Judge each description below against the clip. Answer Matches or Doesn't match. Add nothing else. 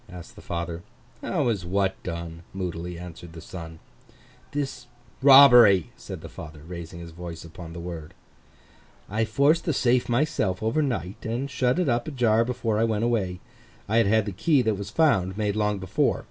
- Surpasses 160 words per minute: Matches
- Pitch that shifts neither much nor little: Doesn't match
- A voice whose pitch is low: Matches